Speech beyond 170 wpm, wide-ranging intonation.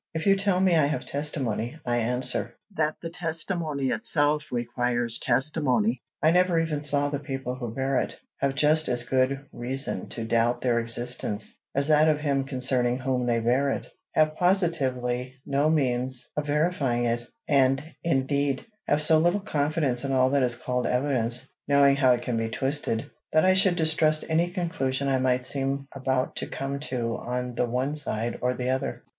No: average, 180 wpm; average, 3.6 semitones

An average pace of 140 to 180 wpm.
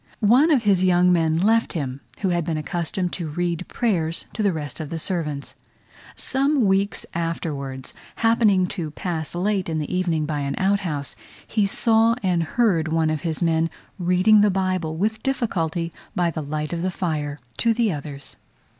Yes: average, 175 wpm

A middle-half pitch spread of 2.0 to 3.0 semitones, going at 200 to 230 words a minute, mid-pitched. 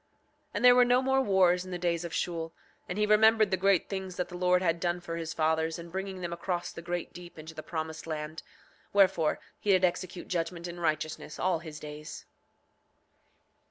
Yes: narrow, 2.4 semitones; fast, 205 wpm; medium, 175 Hz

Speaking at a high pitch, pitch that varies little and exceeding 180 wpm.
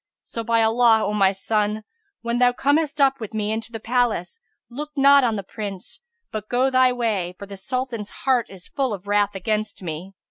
No: high, 225 Hz; average, 3.6 semitones; average, 200 wpm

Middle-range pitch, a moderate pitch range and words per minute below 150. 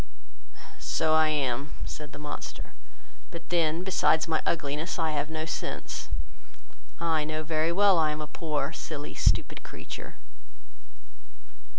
No: medium, 155 Hz; narrow, 1.4 semitones; slow, 135 wpm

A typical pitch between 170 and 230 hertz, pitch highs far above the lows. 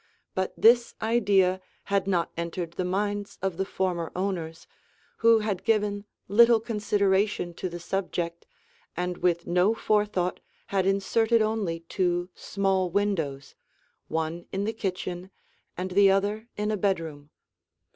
No: high, 190 Hz; average, 2.8 semitones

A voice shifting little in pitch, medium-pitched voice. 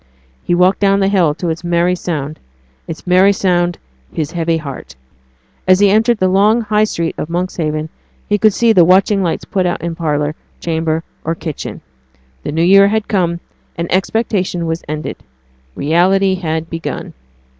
No: average, 3.1 semitones; medium, 175 Hz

